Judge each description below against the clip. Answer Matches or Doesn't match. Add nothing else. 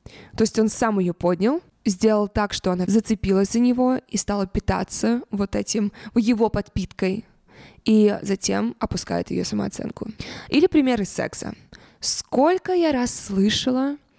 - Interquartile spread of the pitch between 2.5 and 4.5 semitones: Matches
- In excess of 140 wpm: Doesn't match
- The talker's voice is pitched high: Matches